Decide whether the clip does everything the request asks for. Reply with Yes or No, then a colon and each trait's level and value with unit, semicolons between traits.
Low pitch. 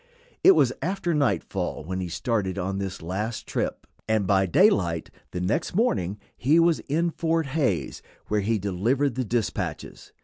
Yes: low, 110 Hz